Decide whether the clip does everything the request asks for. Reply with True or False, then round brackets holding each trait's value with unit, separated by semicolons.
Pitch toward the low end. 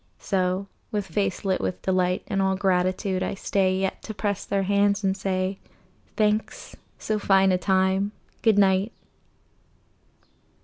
False (195 Hz)